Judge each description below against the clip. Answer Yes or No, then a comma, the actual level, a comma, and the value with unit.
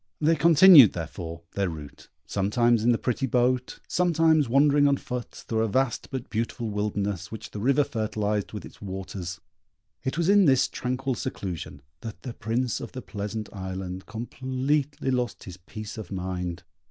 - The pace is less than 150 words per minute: No, average, 165 wpm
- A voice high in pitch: No, low, 115 Hz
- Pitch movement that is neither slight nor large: Yes, average, 5.0 semitones